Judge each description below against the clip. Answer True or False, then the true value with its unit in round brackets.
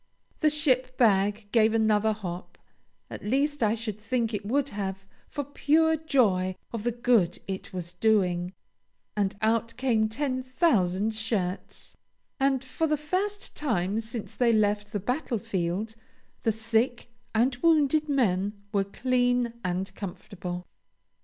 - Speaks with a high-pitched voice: True (225 Hz)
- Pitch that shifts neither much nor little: True (4.4 semitones)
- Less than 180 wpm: True (135 wpm)